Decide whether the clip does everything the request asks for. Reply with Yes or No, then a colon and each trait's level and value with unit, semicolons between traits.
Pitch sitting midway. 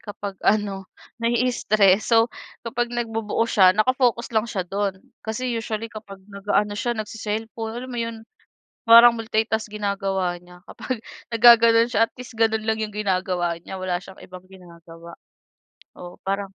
No: high, 215 Hz